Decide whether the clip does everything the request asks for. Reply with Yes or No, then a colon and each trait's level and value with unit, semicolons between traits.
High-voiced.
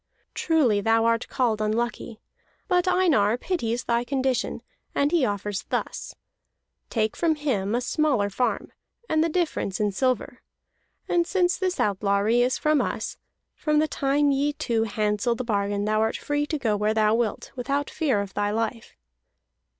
Yes: high, 240 Hz